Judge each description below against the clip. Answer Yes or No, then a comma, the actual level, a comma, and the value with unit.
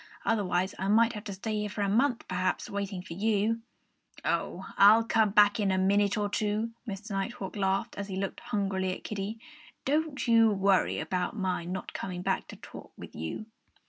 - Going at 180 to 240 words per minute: Yes, average, 190 wpm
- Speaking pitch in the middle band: No, high, 200 Hz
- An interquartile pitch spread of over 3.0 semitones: No, narrow, 2.4 semitones